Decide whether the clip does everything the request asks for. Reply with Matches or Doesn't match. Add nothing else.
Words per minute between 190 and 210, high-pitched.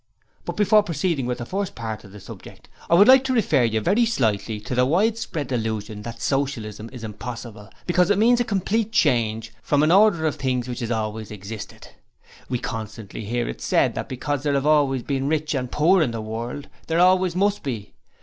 Doesn't match